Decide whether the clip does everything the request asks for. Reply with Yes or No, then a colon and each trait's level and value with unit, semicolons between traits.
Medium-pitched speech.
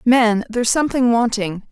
No: high, 230 Hz